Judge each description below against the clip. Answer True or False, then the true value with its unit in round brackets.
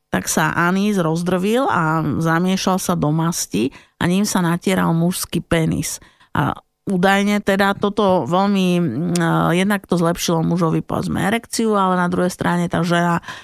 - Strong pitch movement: False (2.5 semitones)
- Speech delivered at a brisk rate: False (145 wpm)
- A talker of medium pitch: True (180 Hz)